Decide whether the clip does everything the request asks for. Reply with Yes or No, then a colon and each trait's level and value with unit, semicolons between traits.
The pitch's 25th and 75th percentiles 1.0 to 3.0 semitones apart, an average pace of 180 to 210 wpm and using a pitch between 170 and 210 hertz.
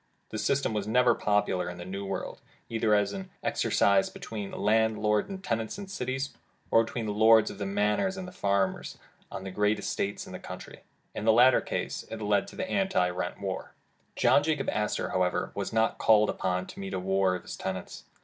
No: average, 2.7 semitones; average, 200 wpm; low, 105 Hz